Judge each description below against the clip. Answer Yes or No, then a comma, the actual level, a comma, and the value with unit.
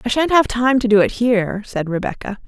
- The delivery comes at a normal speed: No, fast, 240 wpm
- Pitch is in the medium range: No, high, 225 Hz